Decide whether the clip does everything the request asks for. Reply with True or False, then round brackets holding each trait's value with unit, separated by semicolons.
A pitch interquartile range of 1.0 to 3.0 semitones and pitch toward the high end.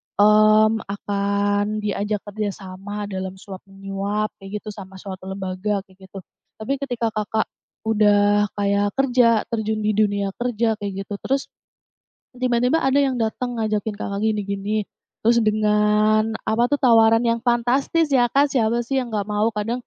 True (2.4 semitones; 215 Hz)